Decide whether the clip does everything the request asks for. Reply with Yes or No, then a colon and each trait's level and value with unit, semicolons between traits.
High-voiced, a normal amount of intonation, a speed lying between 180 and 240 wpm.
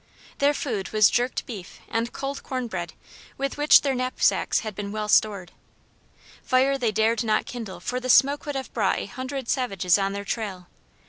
Yes: high, 235 Hz; average, 4.4 semitones; average, 185 wpm